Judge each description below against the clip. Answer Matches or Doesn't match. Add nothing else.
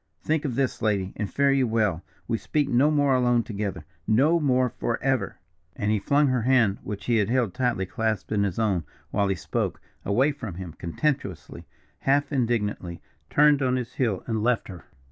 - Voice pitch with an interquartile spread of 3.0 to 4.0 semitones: Doesn't match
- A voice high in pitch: Doesn't match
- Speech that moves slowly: Doesn't match